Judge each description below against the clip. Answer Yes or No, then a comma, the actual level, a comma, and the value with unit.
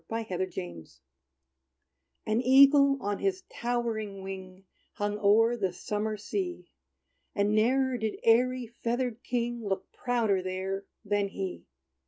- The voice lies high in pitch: Yes, high, 215 Hz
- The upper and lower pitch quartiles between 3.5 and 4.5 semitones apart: Yes, average, 3.9 semitones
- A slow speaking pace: Yes, slow, 130 wpm